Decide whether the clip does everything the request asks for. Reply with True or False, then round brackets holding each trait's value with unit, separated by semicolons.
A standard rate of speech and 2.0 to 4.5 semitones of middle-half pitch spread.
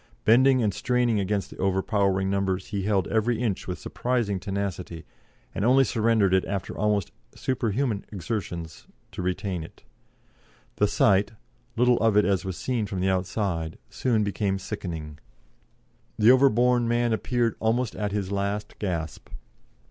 True (145 wpm; 3.5 semitones)